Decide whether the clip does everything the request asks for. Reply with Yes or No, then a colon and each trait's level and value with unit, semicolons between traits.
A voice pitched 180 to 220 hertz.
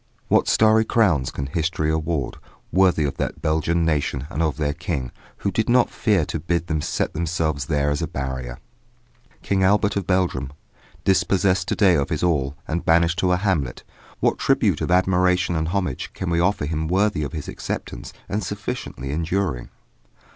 No: very low, 85 Hz